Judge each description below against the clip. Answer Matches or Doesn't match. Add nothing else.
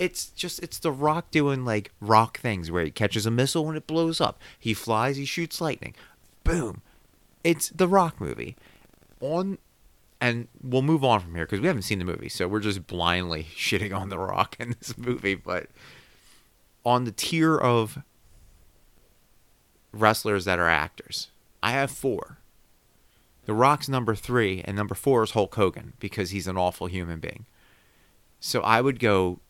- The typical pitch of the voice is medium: Doesn't match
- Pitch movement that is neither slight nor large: Doesn't match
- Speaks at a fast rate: Doesn't match